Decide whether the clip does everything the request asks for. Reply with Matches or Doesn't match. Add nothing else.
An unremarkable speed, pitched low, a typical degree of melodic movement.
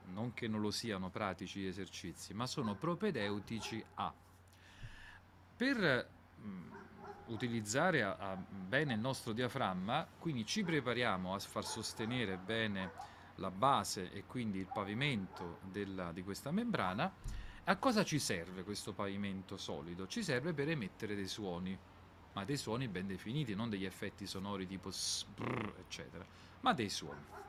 Matches